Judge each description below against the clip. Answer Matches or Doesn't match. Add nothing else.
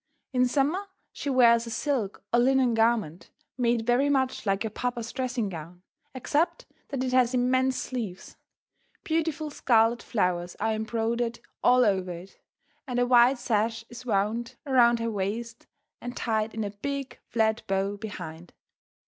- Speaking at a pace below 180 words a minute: Matches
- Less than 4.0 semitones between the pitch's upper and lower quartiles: Matches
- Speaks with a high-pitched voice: Matches